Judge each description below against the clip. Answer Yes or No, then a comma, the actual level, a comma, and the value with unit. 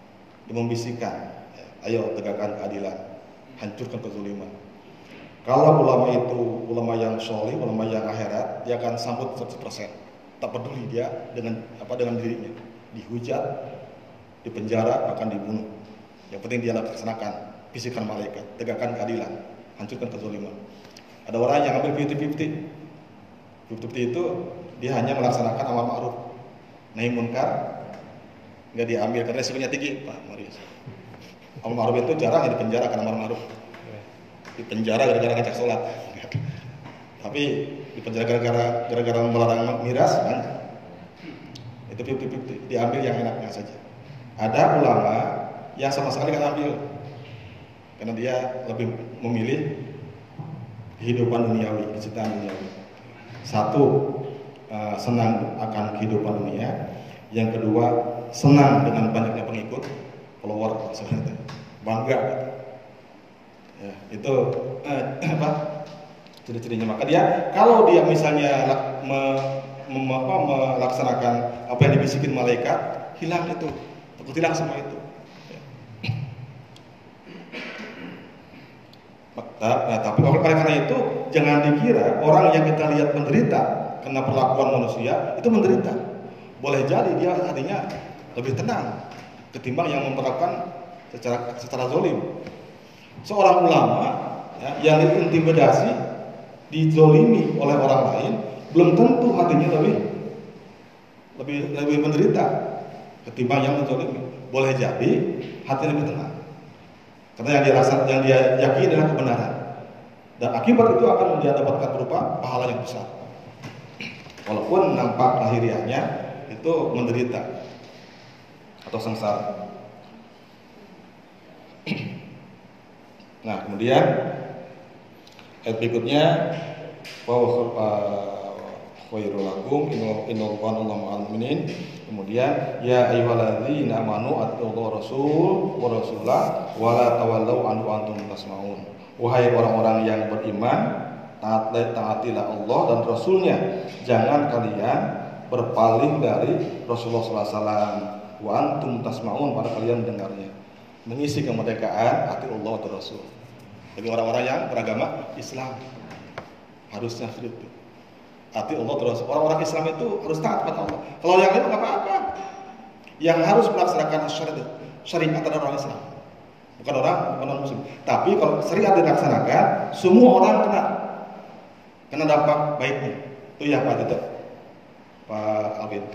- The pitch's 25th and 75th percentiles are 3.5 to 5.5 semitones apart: Yes, average, 4.1 semitones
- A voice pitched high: No, low, 125 Hz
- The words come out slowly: No, average, 110 wpm